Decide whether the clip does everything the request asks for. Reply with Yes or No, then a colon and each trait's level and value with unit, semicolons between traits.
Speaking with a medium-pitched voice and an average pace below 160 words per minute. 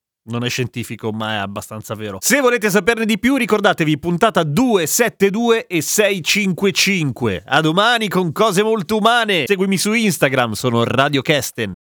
Yes: medium, 180 Hz; average, 145 wpm